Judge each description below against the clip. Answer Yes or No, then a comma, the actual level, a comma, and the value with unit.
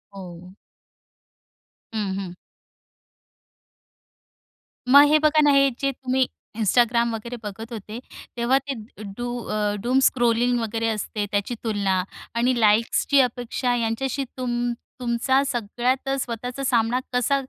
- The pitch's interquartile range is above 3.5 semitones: No, average, 2.8 semitones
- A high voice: Yes, high, 240 Hz